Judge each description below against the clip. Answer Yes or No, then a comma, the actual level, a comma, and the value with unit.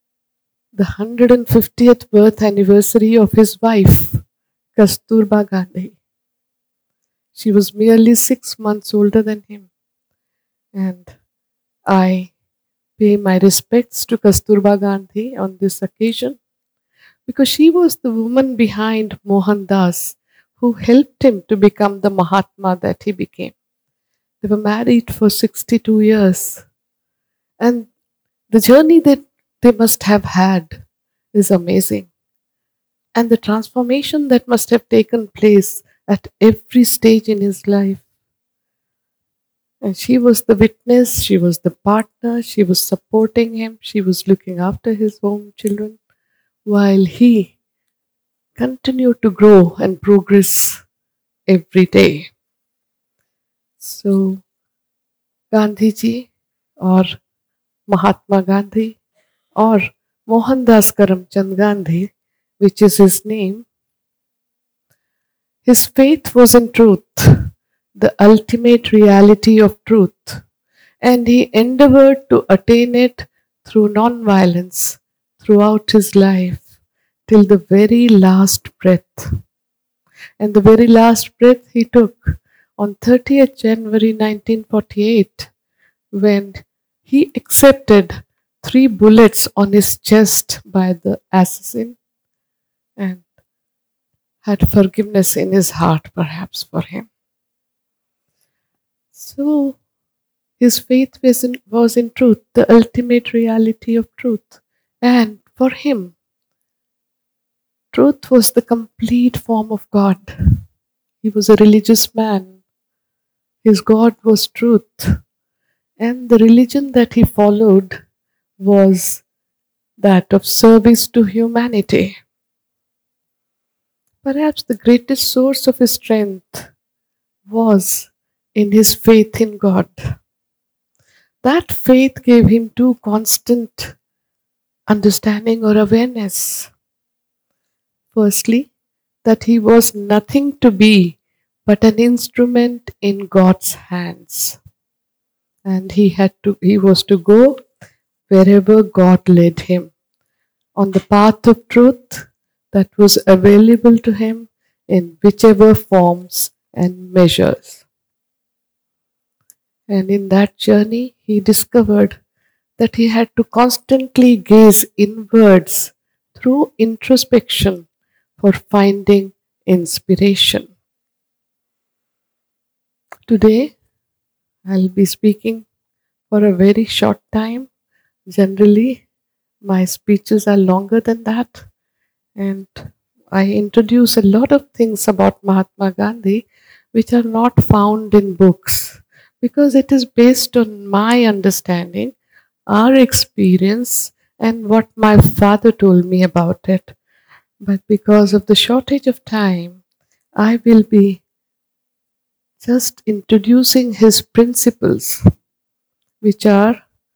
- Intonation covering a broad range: No, average, 3.1 semitones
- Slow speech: Yes, slow, 105 wpm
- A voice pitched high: Yes, high, 215 Hz